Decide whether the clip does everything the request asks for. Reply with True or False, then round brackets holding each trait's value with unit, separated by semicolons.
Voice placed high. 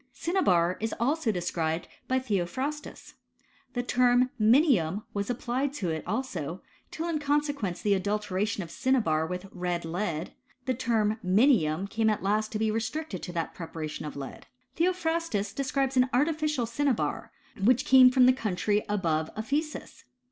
True (220 Hz)